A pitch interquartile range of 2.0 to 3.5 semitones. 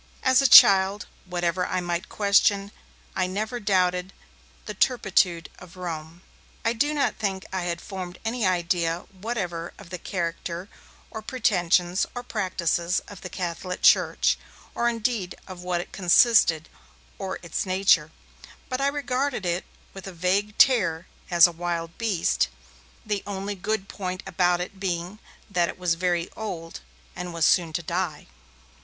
Yes: average, 2.9 semitones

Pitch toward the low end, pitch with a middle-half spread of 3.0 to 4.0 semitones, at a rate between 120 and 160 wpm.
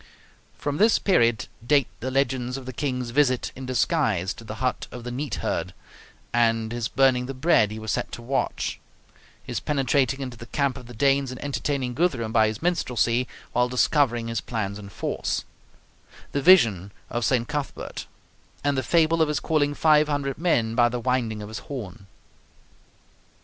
No: low, 125 Hz; average, 3.5 semitones; average, 175 wpm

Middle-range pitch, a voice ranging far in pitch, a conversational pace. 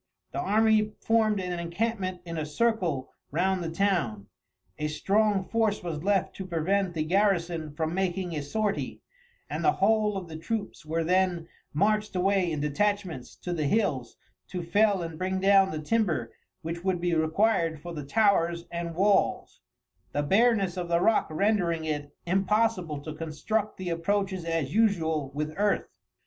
No: medium, 180 Hz; average, 4.0 semitones; average, 160 wpm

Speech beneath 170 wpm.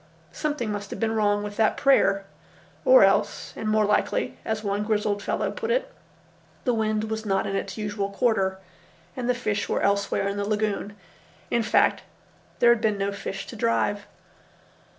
No: average, 175 wpm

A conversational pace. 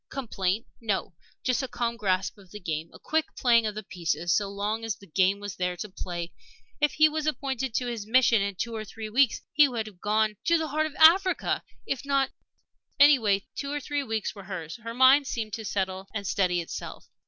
No: fast, 215 wpm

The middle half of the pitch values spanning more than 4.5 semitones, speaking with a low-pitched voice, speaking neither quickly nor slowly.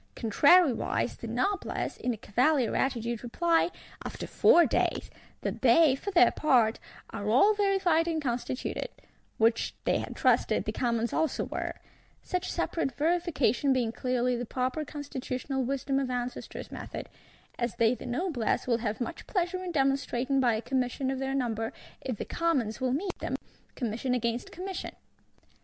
No: average, 5.1 semitones; very high, 260 Hz; average, 150 wpm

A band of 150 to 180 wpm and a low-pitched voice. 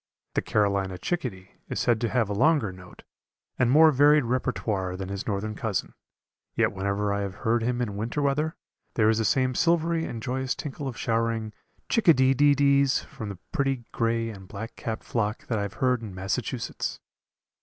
No: average, 190 wpm; low, 115 Hz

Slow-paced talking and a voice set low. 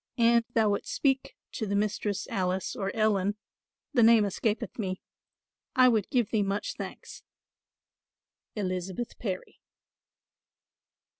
No: slow, 120 wpm; high, 210 Hz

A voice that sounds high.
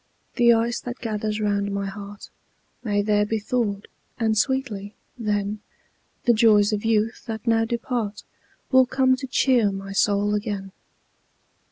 Yes: high, 215 Hz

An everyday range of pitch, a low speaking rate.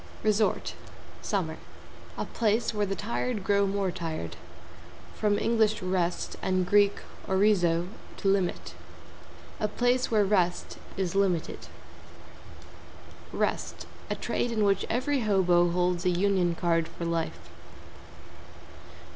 Yes: average, 3.1 semitones; slow, 115 wpm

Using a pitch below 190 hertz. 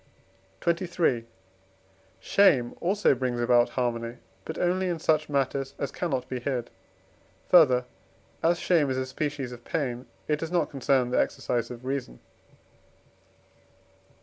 Yes: low, 135 Hz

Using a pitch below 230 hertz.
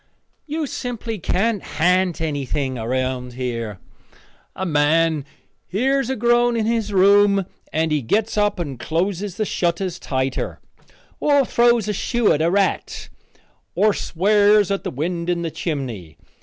Yes: medium, 185 Hz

